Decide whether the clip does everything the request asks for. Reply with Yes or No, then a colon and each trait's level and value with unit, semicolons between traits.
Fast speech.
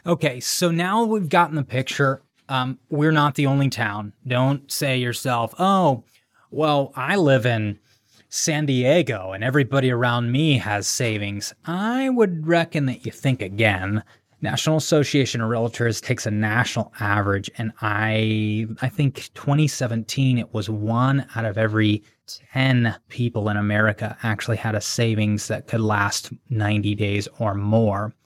No: average, 150 wpm